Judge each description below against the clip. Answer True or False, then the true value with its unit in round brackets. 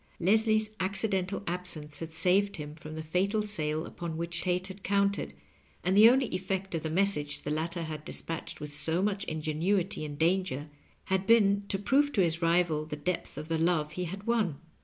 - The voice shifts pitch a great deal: False (4.0 semitones)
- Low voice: False (180 Hz)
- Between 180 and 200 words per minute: True (190 wpm)